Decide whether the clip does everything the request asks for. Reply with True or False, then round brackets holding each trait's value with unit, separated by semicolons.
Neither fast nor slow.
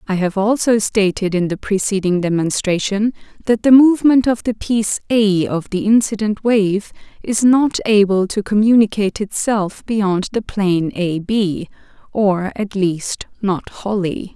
True (145 wpm)